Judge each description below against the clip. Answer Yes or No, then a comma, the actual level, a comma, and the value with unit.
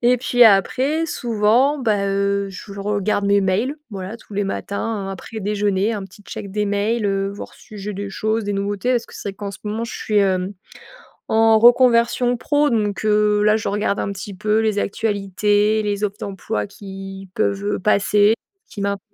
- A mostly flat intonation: Yes, narrow, 1.9 semitones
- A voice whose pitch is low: No, high, 205 Hz